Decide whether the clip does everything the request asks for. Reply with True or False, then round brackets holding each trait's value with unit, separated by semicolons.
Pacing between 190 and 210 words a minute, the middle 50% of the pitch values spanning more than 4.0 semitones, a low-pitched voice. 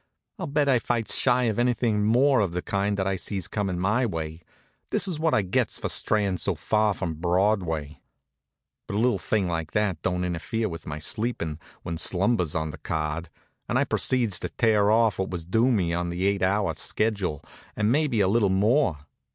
True (200 wpm; 4.5 semitones; 100 Hz)